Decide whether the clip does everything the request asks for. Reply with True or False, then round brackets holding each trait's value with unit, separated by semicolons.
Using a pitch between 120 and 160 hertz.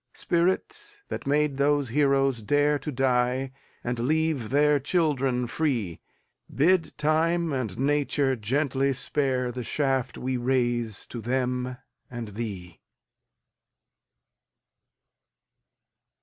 True (135 Hz)